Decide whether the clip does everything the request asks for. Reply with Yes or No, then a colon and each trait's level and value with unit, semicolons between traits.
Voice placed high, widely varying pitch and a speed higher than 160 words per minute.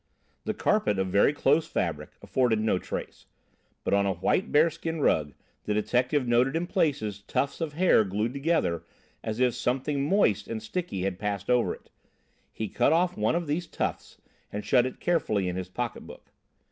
No: low, 125 Hz; wide, 6.9 semitones; average, 175 wpm